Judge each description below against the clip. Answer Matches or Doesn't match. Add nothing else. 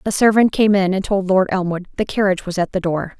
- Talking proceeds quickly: Matches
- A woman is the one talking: Matches